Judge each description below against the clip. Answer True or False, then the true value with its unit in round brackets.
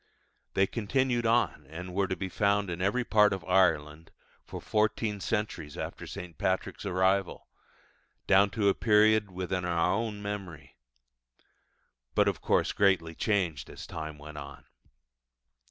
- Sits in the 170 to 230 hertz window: False (95 Hz)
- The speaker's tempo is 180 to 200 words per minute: False (140 wpm)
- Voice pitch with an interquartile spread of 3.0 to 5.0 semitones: True (3.7 semitones)